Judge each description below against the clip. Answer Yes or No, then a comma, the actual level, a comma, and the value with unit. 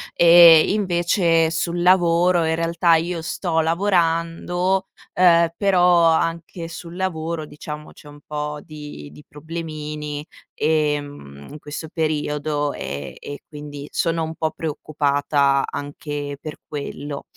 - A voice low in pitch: No, medium, 160 Hz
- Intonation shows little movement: Yes, narrow, 2.3 semitones